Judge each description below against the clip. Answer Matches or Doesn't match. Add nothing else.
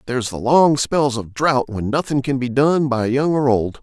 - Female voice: Doesn't match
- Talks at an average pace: Doesn't match